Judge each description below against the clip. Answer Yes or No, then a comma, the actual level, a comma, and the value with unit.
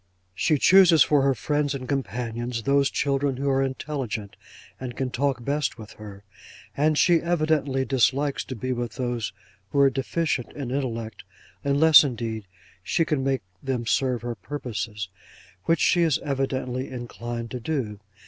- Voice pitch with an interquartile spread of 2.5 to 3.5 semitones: Yes, average, 3.1 semitones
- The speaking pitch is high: No, low, 130 Hz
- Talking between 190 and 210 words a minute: No, average, 155 wpm